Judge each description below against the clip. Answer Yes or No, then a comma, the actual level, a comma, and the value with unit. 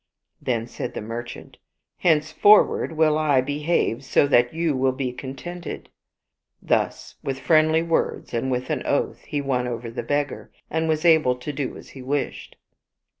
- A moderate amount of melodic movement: Yes, average, 3.8 semitones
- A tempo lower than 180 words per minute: Yes, average, 160 wpm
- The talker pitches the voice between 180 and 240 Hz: No, medium, 140 Hz